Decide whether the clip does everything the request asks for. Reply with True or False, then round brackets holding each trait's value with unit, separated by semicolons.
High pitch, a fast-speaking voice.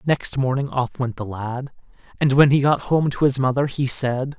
False (135 Hz; 220 wpm)